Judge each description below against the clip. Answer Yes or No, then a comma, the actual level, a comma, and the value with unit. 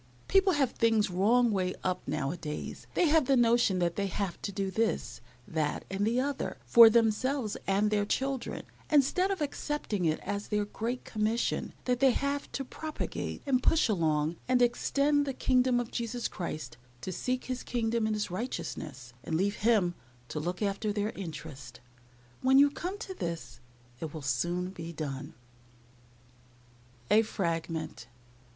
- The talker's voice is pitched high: Yes, high, 215 Hz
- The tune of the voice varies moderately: No, wide, 6.5 semitones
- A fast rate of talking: No, average, 165 wpm